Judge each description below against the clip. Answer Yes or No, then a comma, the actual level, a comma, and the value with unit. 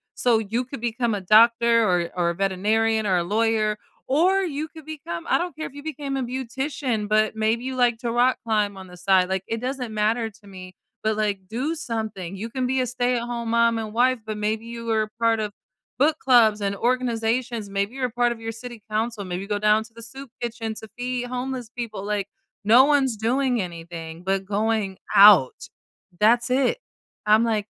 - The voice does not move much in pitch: No, average, 3.0 semitones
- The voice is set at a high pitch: Yes, high, 225 Hz